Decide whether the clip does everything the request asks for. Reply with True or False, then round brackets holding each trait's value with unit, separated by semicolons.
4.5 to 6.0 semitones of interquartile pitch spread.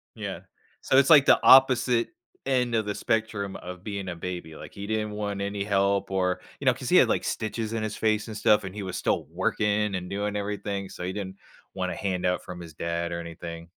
False (2.8 semitones)